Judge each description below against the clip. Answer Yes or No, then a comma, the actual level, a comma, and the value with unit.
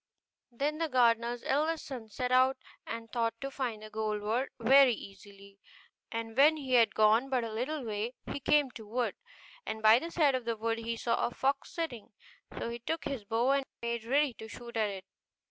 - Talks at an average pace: No, fast, 210 wpm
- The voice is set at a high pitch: Yes, high, 235 Hz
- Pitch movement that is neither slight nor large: Yes, average, 3.4 semitones